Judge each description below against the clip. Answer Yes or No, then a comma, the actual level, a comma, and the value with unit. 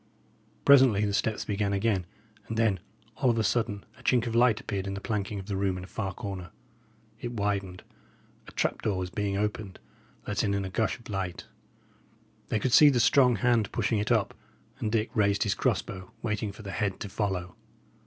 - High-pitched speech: No, low, 105 Hz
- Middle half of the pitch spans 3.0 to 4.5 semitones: No, narrow, 2.6 semitones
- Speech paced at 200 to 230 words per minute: Yes, fast, 205 wpm